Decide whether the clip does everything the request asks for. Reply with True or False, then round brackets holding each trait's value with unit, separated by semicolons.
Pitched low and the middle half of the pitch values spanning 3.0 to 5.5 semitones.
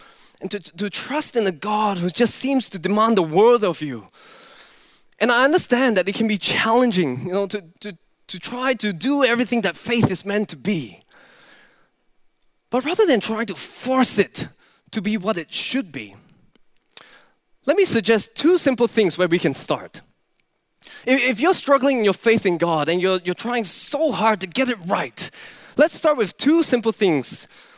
False (220 Hz; 5.2 semitones)